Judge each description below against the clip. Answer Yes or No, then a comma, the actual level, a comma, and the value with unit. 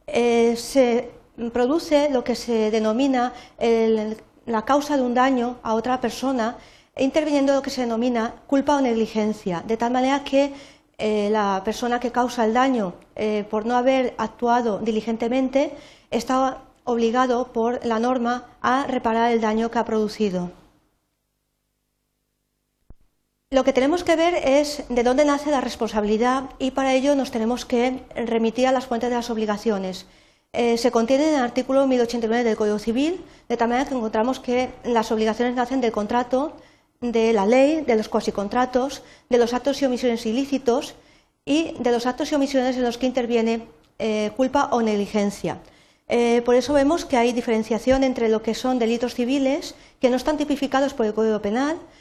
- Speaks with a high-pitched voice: Yes, high, 245 Hz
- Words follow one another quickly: No, average, 165 wpm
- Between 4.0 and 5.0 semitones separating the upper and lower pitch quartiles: No, average, 2.7 semitones